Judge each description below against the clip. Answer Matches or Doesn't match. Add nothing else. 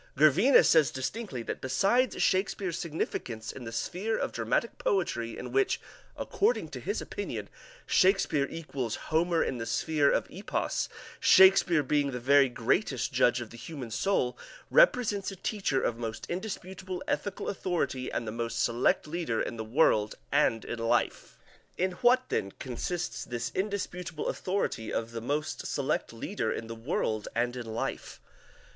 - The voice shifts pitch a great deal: Matches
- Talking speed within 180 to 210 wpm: Doesn't match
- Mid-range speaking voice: Matches